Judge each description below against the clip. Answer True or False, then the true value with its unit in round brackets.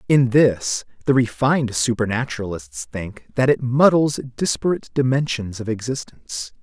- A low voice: True (120 Hz)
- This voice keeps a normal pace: False (120 wpm)